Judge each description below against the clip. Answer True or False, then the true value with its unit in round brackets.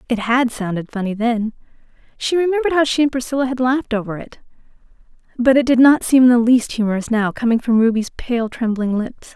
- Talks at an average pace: True (195 wpm)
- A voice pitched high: True (240 Hz)